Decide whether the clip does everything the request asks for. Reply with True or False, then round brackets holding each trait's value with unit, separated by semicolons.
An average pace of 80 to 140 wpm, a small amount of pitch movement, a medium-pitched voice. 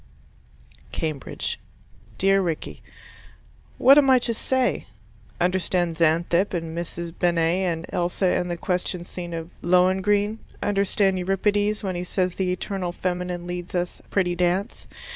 True (135 wpm; 2.0 semitones; 180 Hz)